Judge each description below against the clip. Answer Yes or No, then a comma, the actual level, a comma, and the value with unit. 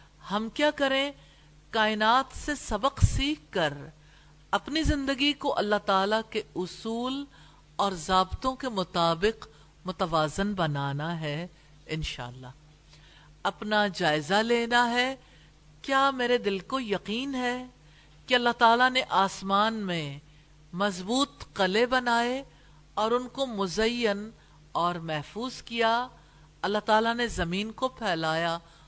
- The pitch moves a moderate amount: No, wide, 6.8 semitones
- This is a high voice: Yes, high, 205 Hz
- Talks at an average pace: No, slow, 115 wpm